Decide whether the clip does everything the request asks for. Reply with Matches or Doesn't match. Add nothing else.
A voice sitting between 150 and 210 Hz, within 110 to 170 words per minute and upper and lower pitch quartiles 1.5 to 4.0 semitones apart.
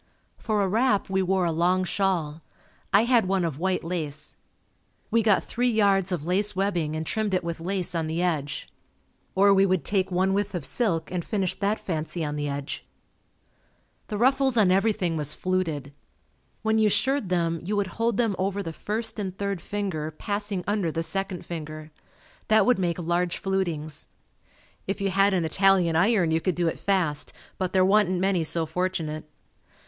Doesn't match